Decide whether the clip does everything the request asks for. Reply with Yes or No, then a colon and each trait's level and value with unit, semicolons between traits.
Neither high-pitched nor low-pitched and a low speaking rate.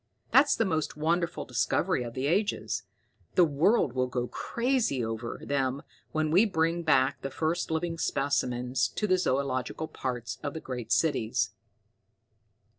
No: medium, 145 Hz; average, 145 wpm